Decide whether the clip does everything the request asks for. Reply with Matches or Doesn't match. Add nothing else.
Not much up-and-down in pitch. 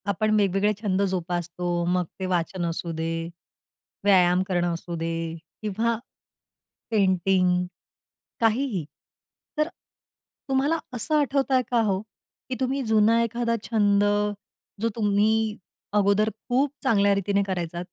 Doesn't match